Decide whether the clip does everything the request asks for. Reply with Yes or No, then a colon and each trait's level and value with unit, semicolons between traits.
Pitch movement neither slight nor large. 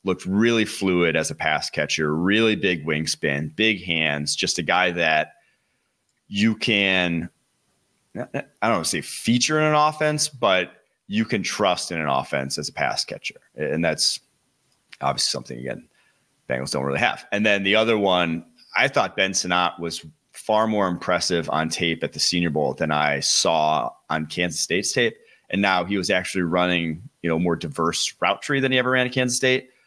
No: wide, 6.0 semitones